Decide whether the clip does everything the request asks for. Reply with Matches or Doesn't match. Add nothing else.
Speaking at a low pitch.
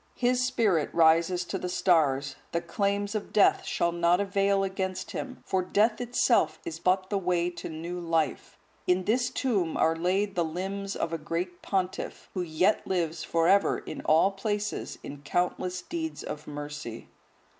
Doesn't match